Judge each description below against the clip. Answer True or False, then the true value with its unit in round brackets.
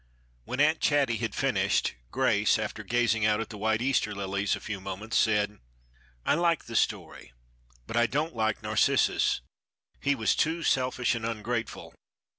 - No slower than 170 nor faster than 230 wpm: False (160 wpm)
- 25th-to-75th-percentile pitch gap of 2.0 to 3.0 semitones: False (3.5 semitones)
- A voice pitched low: True (115 Hz)